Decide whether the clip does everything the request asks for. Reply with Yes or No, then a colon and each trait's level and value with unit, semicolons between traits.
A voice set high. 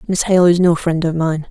No: medium, 170 Hz